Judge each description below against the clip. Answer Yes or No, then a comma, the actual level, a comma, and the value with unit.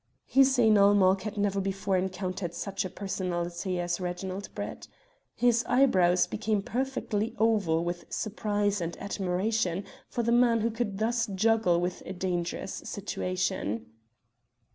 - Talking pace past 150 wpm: No, slow, 135 wpm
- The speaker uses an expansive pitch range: No, average, 3.4 semitones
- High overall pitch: Yes, high, 195 Hz